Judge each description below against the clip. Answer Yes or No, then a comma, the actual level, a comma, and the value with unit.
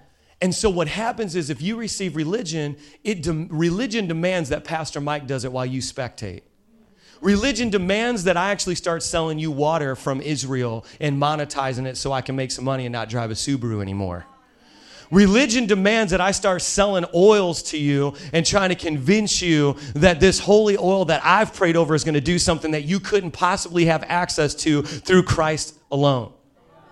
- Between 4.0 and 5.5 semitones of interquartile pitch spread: Yes, average, 5.0 semitones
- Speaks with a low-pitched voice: No, medium, 165 Hz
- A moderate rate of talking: Yes, average, 185 wpm